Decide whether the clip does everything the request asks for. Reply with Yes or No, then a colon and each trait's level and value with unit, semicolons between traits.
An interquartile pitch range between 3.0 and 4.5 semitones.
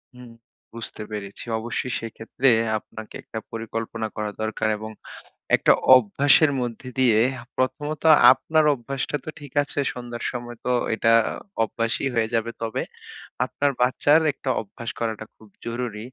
No: narrow, 2.6 semitones